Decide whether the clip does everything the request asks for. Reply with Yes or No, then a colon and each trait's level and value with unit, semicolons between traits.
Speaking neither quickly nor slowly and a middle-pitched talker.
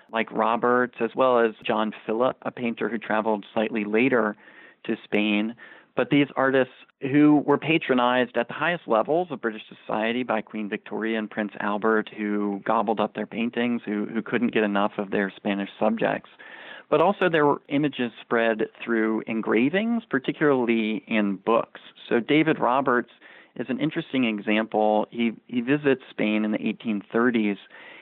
No: average, 155 wpm; low, 115 Hz